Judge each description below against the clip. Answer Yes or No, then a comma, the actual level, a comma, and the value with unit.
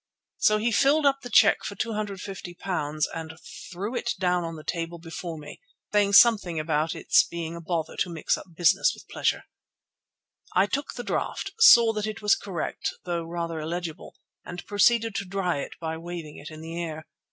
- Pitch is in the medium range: Yes, medium, 175 Hz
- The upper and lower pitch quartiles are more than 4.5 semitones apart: No, average, 4.1 semitones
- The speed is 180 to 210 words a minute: Yes, average, 185 wpm